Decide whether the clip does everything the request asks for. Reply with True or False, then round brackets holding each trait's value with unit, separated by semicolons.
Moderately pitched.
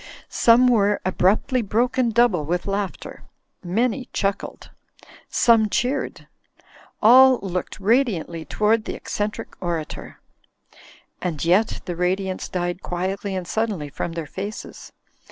False (200 Hz)